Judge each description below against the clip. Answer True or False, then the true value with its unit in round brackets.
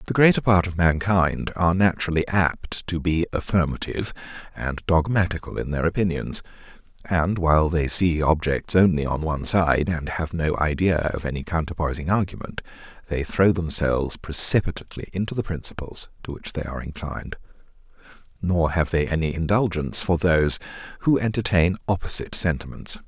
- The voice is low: True (85 Hz)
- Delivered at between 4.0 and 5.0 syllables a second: False (5.5 syllables/s)